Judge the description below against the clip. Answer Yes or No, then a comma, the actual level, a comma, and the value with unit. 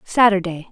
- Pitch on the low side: No, high, 190 Hz